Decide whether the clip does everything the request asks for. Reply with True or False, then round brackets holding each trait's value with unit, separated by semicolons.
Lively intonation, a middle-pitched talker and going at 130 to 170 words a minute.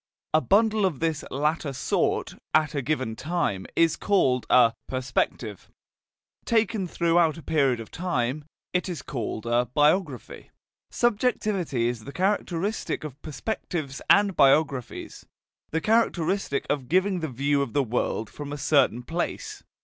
True (5.7 semitones; 155 Hz; 140 wpm)